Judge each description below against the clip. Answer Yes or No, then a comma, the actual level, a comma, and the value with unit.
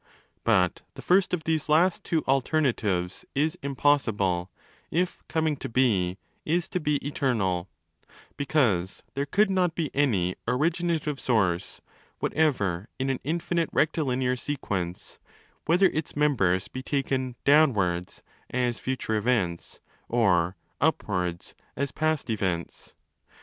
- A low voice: Yes, low, 130 Hz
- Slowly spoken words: Yes, slow, 120 wpm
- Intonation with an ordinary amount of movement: No, wide, 8.2 semitones